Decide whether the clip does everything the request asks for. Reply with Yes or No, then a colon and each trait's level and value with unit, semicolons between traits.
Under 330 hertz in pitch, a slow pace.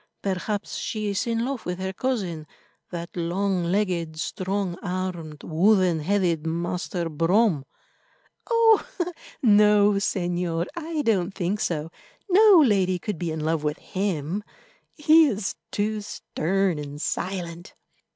Yes: medium, 185 Hz; slow, 120 wpm